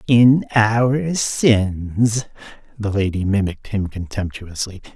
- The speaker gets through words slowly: Yes, slow, 95 wpm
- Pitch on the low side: Yes, low, 105 Hz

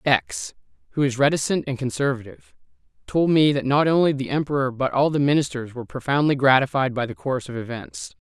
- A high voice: No, low, 135 Hz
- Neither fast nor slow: Yes, average, 180 wpm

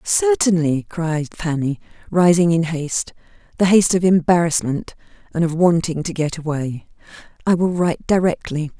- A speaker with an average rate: No, slow, 130 wpm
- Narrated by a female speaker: Yes, female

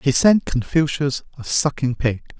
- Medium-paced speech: Yes, average, 150 wpm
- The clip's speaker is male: Yes, male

